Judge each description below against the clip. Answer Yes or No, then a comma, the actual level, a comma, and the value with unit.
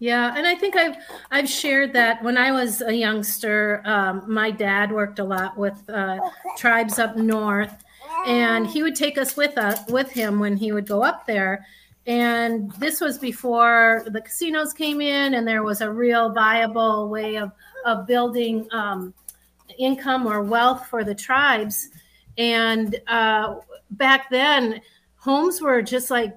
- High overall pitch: Yes, high, 230 Hz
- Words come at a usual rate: Yes, average, 165 wpm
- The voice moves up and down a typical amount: Yes, average, 3.4 semitones